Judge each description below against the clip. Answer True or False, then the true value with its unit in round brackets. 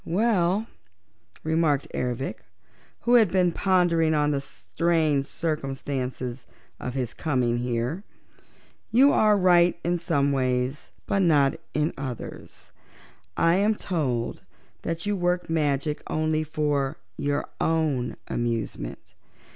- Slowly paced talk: True (115 wpm)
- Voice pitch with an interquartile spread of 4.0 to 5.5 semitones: True (4.4 semitones)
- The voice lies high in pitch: False (155 Hz)